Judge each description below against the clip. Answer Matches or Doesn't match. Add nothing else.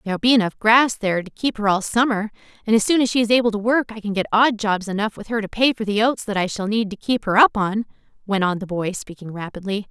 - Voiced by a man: Doesn't match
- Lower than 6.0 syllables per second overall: Doesn't match